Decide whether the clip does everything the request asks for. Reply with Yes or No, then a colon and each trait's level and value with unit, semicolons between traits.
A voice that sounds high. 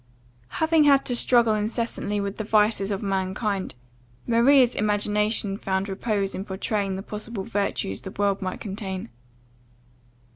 Yes: high, 205 Hz